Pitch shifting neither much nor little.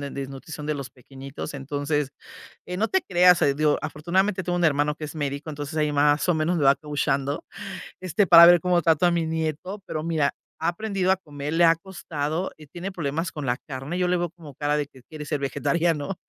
Yes: average, 3.3 semitones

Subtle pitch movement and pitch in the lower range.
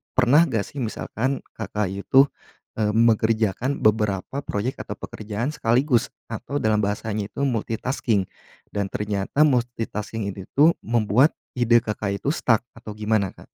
No: average, 3.1 semitones; low, 110 Hz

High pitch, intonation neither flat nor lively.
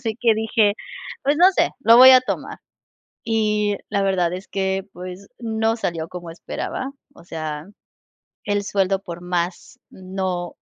Yes: high, 195 Hz; average, 3.8 semitones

